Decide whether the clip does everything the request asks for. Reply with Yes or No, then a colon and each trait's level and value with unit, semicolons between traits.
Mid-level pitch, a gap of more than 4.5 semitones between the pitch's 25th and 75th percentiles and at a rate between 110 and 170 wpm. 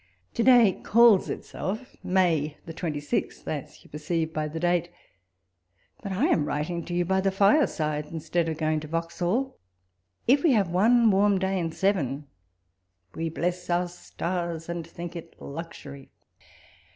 No: medium, 175 Hz; average, 3.4 semitones; average, 165 wpm